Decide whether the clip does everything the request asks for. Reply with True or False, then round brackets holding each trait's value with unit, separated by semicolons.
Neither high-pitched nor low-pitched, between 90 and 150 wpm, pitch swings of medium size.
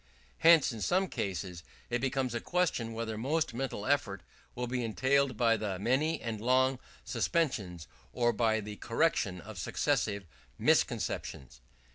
False (120 Hz; 140 wpm; 4.3 semitones)